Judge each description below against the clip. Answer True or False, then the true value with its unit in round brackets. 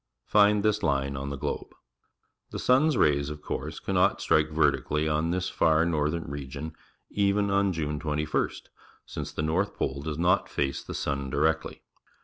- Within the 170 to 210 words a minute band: False (160 wpm)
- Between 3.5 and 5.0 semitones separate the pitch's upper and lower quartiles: True (4.1 semitones)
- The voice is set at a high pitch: False (80 Hz)